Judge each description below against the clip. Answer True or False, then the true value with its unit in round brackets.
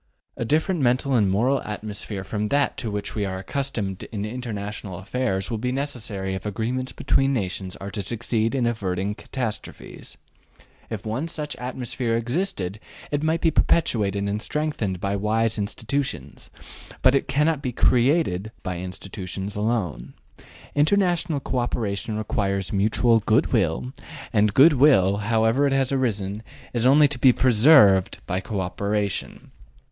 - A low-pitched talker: True (110 Hz)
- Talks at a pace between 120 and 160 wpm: True (150 wpm)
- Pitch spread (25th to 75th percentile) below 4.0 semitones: False (4.9 semitones)